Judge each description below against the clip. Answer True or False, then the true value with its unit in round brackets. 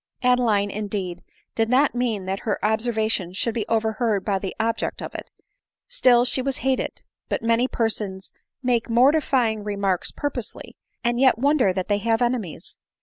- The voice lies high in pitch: True (225 Hz)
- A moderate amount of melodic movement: True (3.3 semitones)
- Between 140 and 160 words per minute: False (175 wpm)